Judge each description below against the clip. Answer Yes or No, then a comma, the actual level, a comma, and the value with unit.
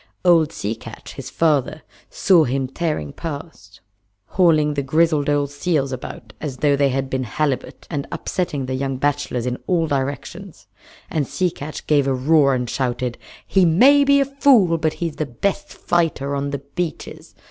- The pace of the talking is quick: No, average, 175 wpm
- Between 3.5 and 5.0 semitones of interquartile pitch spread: Yes, average, 3.8 semitones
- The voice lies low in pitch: No, medium, 145 Hz